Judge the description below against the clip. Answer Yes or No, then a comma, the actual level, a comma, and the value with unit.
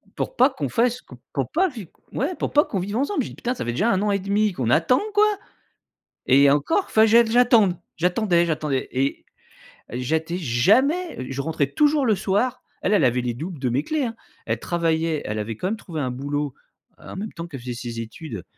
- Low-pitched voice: No, medium, 175 Hz